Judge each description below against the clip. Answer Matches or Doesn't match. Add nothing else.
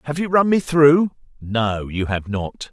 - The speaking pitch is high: Doesn't match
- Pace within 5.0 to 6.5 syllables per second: Doesn't match